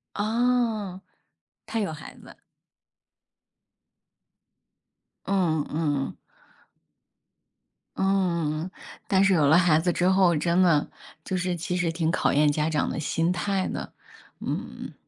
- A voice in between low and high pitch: Yes, medium, 175 Hz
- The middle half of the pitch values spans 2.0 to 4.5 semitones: Yes, average, 3.3 semitones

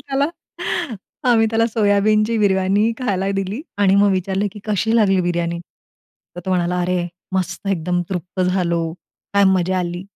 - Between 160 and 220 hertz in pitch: Yes, high, 190 Hz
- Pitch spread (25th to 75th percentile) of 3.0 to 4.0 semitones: No, narrow, 2.6 semitones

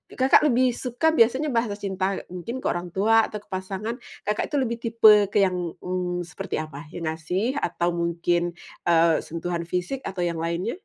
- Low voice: No, high, 190 Hz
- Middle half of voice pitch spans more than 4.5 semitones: Yes, average, 4.9 semitones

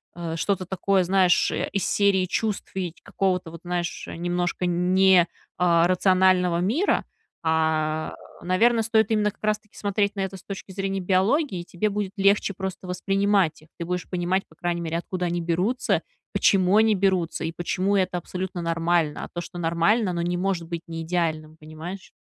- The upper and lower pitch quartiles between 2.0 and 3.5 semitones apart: Yes, narrow, 2.4 semitones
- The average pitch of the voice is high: No, medium, 180 Hz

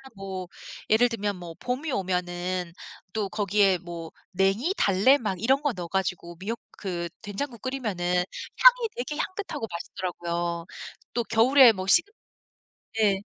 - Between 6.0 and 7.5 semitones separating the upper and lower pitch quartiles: No, average, 5.3 semitones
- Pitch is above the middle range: Yes, high, 195 Hz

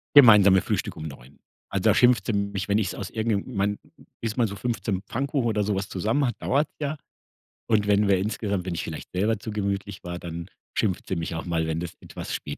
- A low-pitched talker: Yes, low, 100 Hz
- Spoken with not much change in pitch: No, average, 3.4 semitones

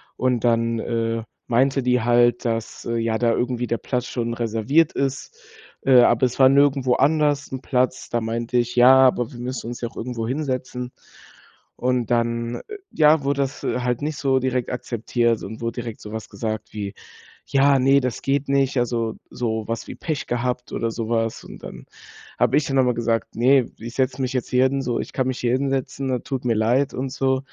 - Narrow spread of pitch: Yes, narrow, 2.3 semitones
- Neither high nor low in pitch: No, low, 125 Hz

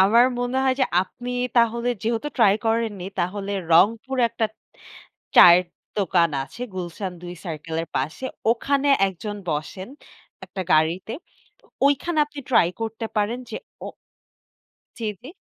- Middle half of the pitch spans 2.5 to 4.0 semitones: No, average, 5.3 semitones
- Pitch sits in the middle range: No, high, 215 Hz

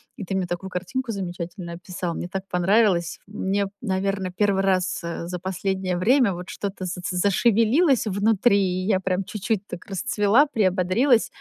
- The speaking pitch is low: No, high, 190 Hz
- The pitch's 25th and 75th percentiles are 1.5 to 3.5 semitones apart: Yes, narrow, 2.5 semitones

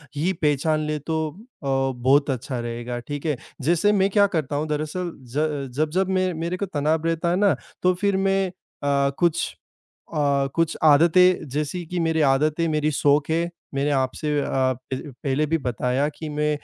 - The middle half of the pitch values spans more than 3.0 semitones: Yes, average, 3.4 semitones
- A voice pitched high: No, medium, 155 Hz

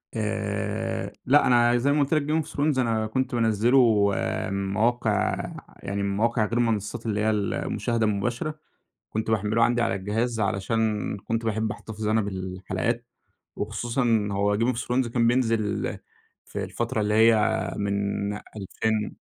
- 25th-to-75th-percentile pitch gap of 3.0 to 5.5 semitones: No, narrow, 2.6 semitones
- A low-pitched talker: Yes, low, 110 Hz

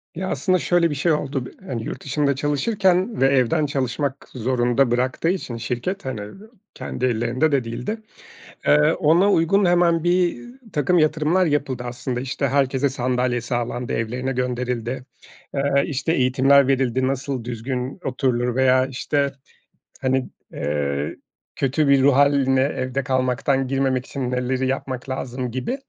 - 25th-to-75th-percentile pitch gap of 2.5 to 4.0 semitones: Yes, average, 2.9 semitones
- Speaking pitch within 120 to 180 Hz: Yes, low, 135 Hz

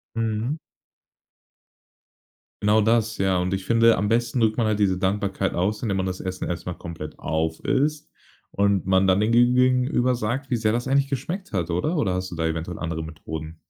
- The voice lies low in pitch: Yes, low, 105 Hz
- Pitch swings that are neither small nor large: Yes, average, 4.6 semitones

